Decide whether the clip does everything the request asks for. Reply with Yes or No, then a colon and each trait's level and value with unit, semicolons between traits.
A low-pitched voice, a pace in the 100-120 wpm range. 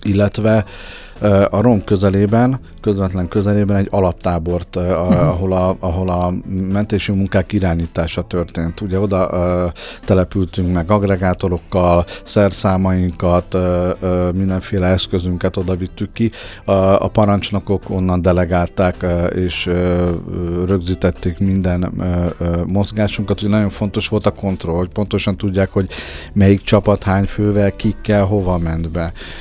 Yes: very low, 95 Hz; average, 110 wpm